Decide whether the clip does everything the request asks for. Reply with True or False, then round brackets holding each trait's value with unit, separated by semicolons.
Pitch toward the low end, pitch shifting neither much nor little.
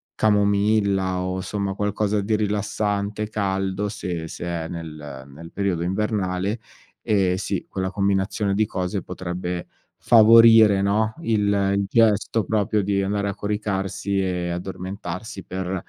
False (100 Hz; 2.1 semitones)